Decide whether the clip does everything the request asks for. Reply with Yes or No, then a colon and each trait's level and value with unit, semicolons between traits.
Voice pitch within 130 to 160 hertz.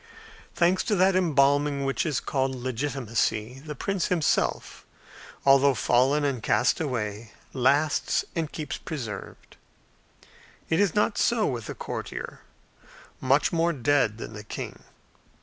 Yes: medium, 140 Hz